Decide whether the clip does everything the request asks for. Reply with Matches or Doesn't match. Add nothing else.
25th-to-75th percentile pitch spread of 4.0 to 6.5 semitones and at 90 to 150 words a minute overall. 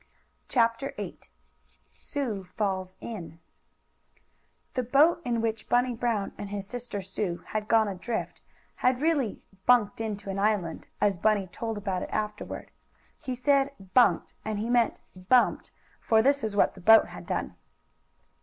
Doesn't match